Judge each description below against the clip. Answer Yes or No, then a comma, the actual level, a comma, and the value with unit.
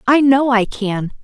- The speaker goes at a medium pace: Yes, average, 195 wpm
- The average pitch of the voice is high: Yes, high, 240 Hz